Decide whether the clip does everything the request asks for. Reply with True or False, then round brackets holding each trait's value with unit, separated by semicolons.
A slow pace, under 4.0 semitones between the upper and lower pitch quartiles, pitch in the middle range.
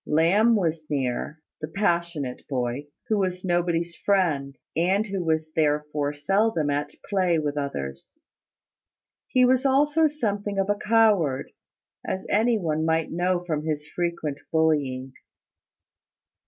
False (125 wpm; 5.1 semitones; 165 Hz)